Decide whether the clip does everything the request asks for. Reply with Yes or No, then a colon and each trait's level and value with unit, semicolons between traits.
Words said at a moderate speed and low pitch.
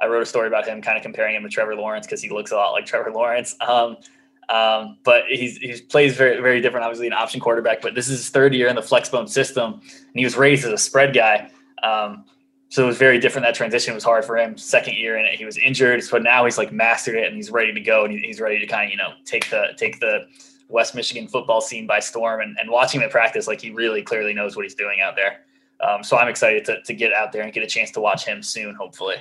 No: fast, 275 wpm; low, 120 Hz